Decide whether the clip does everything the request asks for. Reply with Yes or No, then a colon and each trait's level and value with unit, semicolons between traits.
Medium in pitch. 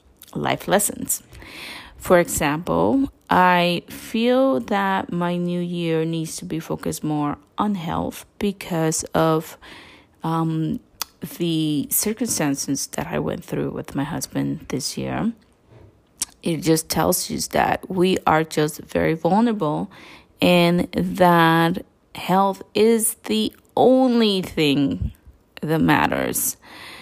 Yes: medium, 175 Hz